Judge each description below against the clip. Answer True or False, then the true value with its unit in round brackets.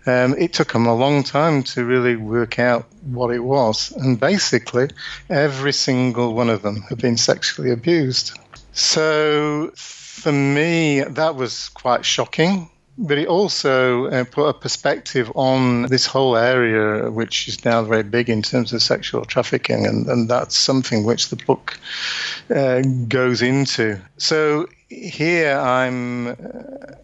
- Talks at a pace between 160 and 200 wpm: False (150 wpm)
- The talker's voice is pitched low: True (130 Hz)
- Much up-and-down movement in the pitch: False (3.3 semitones)